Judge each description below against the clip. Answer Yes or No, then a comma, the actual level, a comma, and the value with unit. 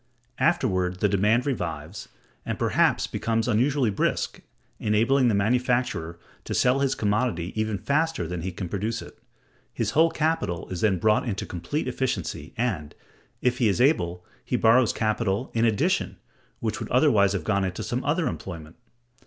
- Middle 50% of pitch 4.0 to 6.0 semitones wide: Yes, average, 5.3 semitones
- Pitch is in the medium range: No, low, 110 Hz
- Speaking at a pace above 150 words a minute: Yes, average, 160 wpm